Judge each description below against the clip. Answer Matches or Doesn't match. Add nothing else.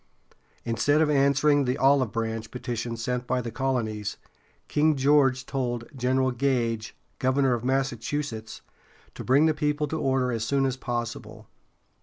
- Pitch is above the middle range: Doesn't match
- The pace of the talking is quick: Doesn't match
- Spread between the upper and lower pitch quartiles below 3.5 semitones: Matches